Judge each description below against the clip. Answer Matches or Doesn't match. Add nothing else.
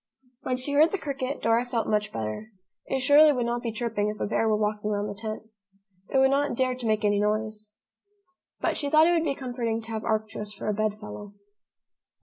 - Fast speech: Matches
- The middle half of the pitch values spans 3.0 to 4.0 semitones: Matches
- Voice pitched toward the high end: Matches